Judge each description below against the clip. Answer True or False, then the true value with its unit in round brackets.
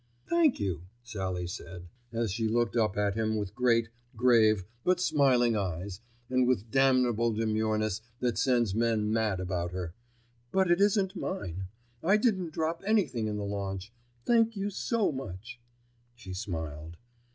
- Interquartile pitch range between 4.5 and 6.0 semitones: True (5.4 semitones)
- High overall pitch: False (115 Hz)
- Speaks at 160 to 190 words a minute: False (150 wpm)